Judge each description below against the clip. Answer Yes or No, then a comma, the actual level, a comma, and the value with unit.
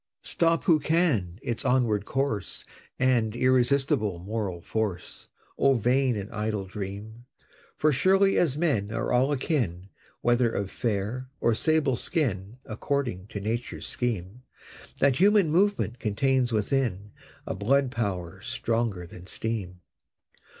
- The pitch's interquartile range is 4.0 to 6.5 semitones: Yes, average, 5.0 semitones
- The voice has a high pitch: No, low, 115 Hz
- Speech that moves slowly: Yes, slow, 125 wpm